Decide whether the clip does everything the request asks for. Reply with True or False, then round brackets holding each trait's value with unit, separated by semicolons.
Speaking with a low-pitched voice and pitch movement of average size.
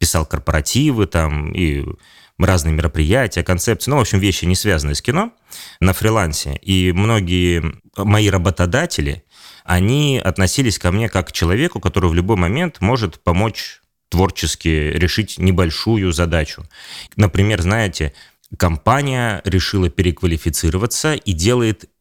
True (95 Hz; 3.8 semitones)